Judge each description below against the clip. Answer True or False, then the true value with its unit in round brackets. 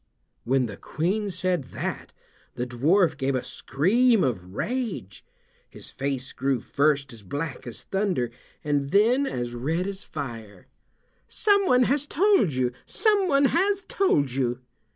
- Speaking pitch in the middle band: True (150 Hz)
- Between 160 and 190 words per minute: False (135 wpm)